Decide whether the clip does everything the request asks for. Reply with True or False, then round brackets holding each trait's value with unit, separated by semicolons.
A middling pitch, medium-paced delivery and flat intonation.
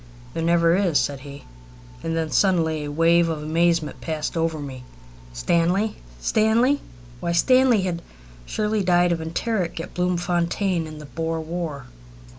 True (170 Hz; 145 wpm; 2.3 semitones)